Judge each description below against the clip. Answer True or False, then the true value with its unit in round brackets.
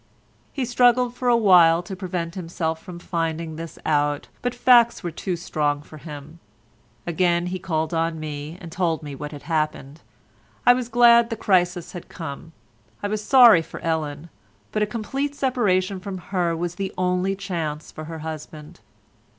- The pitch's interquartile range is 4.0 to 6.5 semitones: True (4.3 semitones)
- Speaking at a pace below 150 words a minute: False (170 wpm)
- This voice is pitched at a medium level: True (175 Hz)